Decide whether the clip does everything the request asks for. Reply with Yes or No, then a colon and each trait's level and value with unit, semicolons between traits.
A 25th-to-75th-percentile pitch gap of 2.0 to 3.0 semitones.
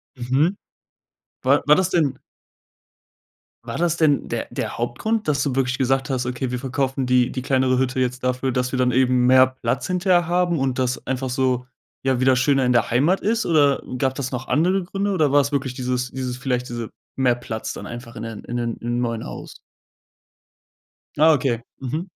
Yes: narrow, 2.6 semitones